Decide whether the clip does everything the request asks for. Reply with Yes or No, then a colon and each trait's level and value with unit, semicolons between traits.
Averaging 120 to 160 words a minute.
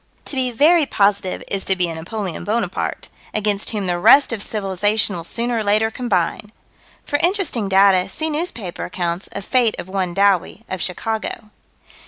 No: average, 170 wpm